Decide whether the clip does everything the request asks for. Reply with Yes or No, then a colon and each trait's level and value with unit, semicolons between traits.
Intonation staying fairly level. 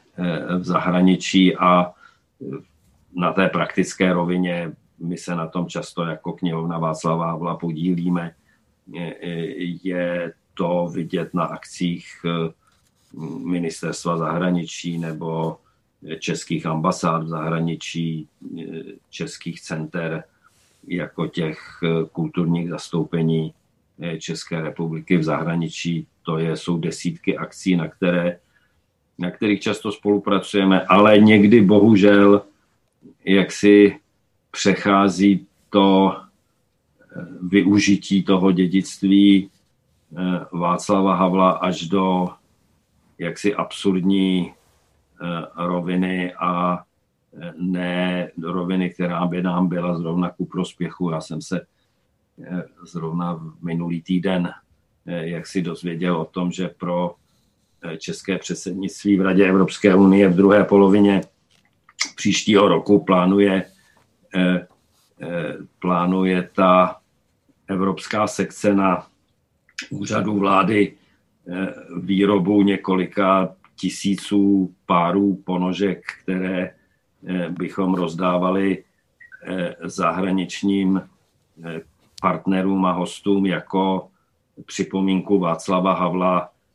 Yes: narrow, 1.9 semitones